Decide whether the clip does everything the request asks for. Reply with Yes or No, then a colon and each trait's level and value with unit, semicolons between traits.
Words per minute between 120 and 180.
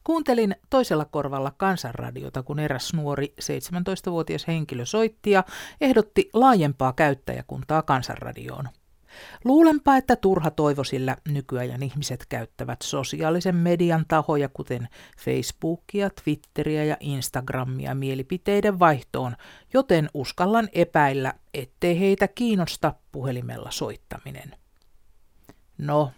No: slow, 95 wpm